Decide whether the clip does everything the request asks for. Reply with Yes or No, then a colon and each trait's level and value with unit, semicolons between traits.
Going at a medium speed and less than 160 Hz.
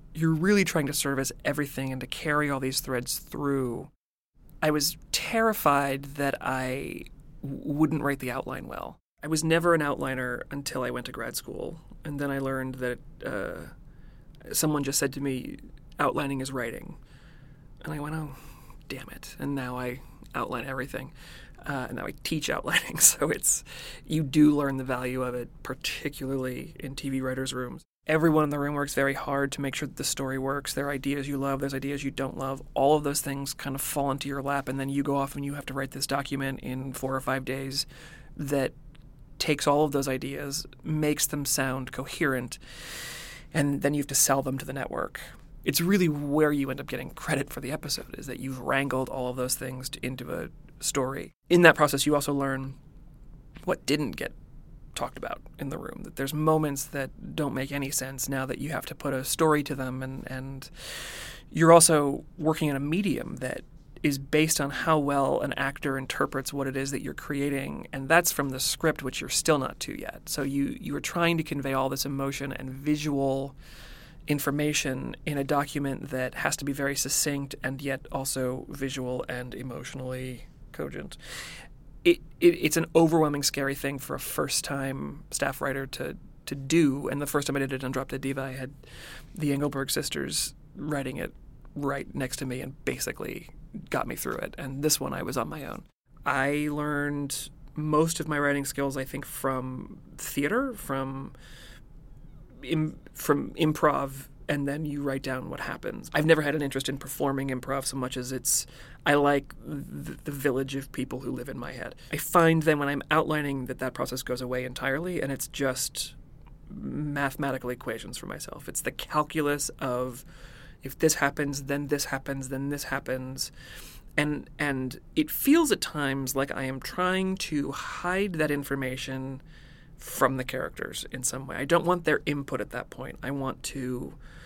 Yes: average, 190 wpm; medium, 140 Hz